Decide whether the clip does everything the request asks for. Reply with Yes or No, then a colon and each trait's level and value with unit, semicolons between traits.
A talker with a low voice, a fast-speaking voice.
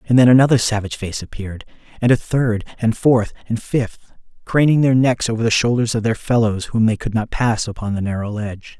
Yes: low, 115 Hz; fast, 210 wpm